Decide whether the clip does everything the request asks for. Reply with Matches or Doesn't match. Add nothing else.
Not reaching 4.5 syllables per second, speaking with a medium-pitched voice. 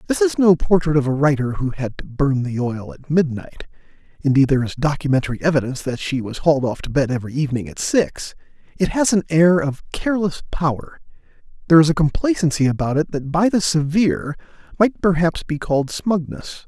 Matches